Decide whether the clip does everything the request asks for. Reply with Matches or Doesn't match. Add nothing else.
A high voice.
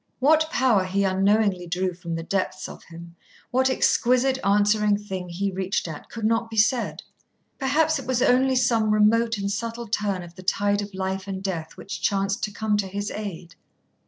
Matches